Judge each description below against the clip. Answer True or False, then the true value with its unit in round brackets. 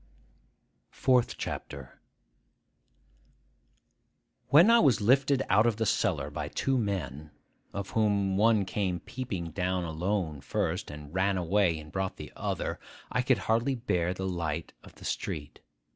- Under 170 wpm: True (140 wpm)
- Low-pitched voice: True (95 Hz)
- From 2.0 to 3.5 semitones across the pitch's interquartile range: False (5.1 semitones)